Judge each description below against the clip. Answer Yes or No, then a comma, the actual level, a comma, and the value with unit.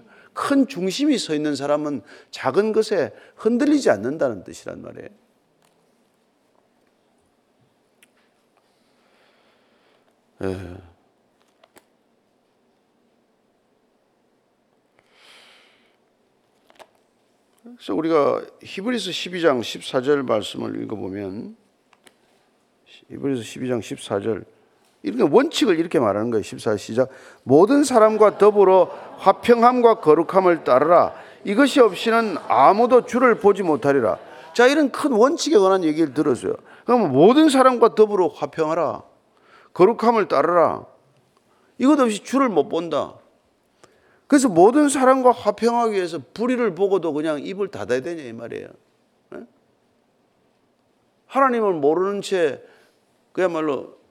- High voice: Yes, high, 210 Hz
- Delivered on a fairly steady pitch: No, wide, 8.0 semitones